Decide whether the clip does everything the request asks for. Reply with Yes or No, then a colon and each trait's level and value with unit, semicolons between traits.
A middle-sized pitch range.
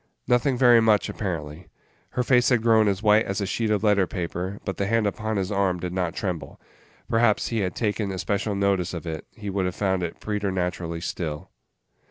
Yes: average, 3.1 semitones